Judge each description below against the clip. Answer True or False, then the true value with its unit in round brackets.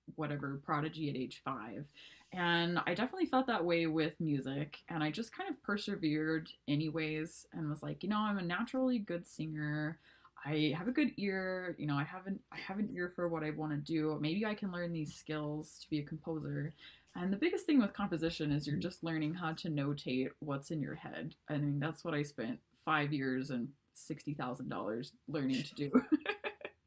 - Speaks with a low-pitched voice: False (155 Hz)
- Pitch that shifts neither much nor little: True (3.5 semitones)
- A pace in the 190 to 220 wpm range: True (205 wpm)